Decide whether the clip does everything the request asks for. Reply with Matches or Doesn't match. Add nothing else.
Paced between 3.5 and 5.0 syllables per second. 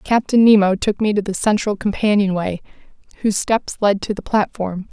Doesn't match